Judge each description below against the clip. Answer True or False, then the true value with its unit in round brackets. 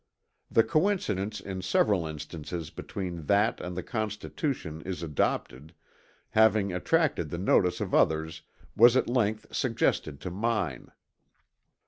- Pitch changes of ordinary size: True (4.9 semitones)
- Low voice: True (95 Hz)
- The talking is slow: True (120 wpm)